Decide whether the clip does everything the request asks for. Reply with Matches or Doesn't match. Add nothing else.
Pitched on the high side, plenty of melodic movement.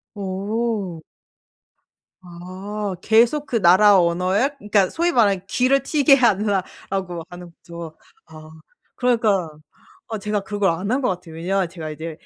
Doesn't match